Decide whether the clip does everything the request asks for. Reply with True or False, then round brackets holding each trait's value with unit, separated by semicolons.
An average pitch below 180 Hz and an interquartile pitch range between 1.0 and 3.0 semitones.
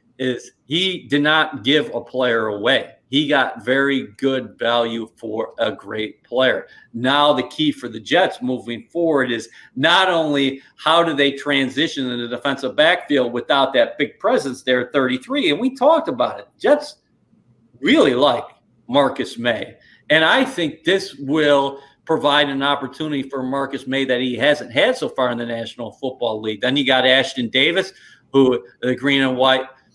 True (135 Hz; 2.7 semitones)